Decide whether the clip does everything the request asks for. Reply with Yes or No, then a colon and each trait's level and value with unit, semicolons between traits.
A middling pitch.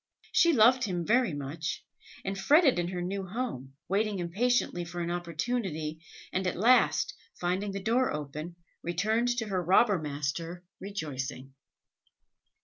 Yes: medium, 180 Hz